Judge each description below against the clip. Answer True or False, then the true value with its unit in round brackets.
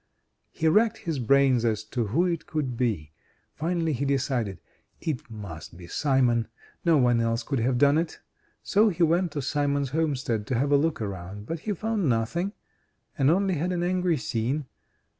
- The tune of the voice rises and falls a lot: True (6.1 semitones)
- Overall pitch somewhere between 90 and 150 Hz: True (140 Hz)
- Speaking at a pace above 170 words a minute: True (180 wpm)